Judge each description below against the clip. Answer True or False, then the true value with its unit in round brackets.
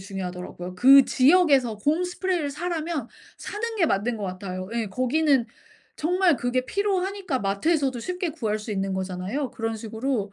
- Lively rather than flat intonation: True (8.4 semitones)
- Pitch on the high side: True (255 Hz)